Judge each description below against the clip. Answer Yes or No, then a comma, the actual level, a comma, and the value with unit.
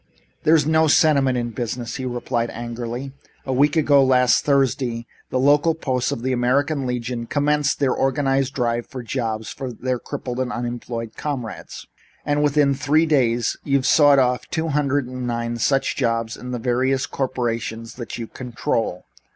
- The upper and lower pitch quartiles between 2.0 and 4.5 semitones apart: Yes, average, 2.8 semitones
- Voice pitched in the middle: No, low, 130 Hz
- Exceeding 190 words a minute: No, average, 165 wpm